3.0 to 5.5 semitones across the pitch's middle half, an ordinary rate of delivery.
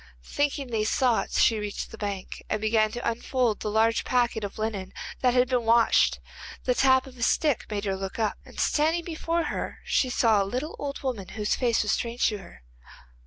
No: average, 3.3 semitones; fast, 210 wpm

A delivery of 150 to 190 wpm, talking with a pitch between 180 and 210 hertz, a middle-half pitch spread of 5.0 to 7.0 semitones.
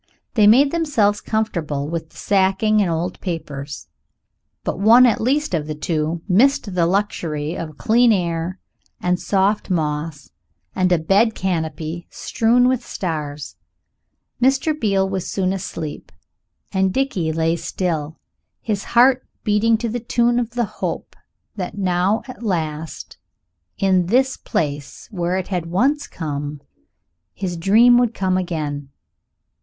No: average, 140 wpm; medium, 185 Hz; wide, 5.4 semitones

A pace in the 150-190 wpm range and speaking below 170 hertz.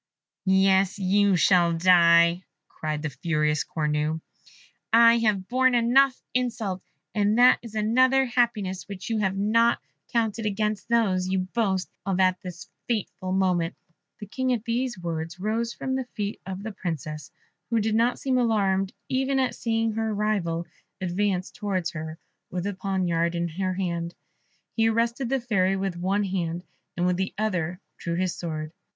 No: average, 160 wpm; high, 195 Hz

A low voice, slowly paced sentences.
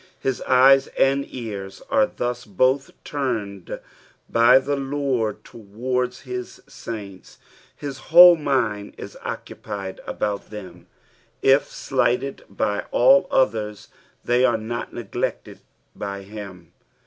Yes: low, 120 Hz; slow, 110 wpm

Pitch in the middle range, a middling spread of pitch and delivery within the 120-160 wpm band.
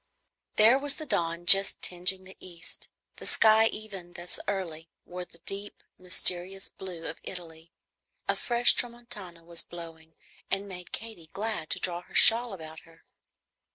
Yes: medium, 180 Hz; average, 3.8 semitones; average, 155 wpm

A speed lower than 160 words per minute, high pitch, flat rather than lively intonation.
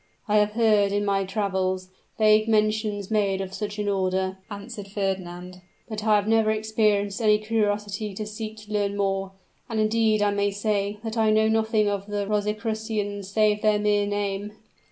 No: average, 170 wpm; high, 210 Hz; narrow, 1.3 semitones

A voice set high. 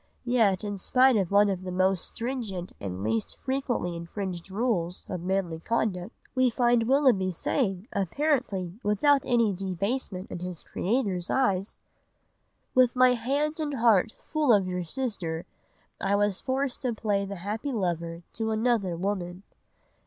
Yes: high, 200 Hz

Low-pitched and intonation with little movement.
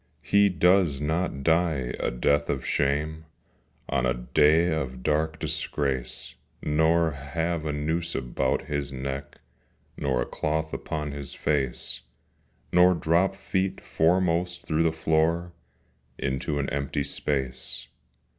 No: very low, 75 Hz; average, 3.3 semitones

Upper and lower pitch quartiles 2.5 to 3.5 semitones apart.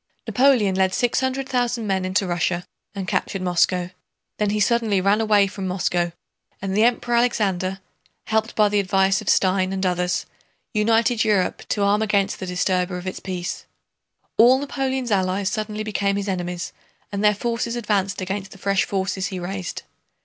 Yes: average, 2.8 semitones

